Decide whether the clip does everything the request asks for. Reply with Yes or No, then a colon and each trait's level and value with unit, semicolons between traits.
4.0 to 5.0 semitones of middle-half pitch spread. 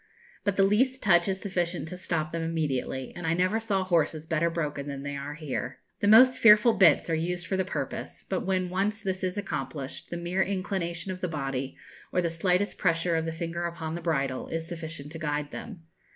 No: average, 3.1 semitones